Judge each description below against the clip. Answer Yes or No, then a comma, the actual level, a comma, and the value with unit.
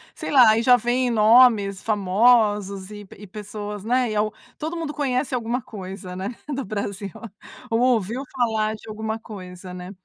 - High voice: Yes, high, 215 Hz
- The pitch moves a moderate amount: Yes, average, 3.4 semitones